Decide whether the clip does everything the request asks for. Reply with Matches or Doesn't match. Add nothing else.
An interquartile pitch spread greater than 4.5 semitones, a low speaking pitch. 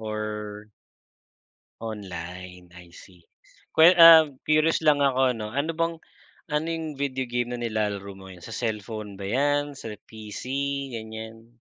Matches